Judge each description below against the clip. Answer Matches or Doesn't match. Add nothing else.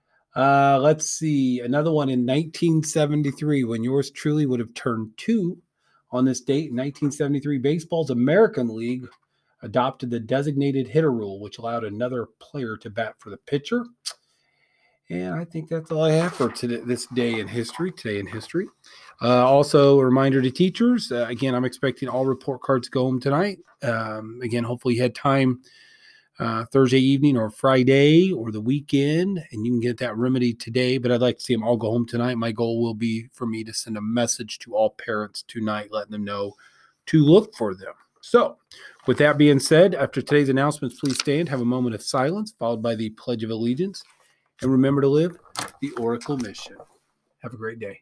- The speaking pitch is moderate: Doesn't match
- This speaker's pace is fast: Doesn't match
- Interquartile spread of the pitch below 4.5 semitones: Matches